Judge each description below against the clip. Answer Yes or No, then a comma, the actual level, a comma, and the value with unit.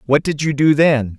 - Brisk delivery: Yes, fast, 255 wpm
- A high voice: No, medium, 145 Hz